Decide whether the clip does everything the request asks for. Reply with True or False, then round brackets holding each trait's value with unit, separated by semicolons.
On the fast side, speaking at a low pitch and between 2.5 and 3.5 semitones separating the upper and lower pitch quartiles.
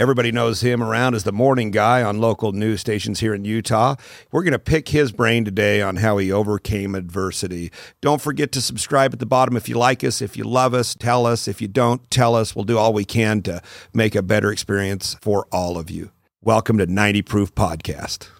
True (220 wpm; 110 Hz; 2.9 semitones)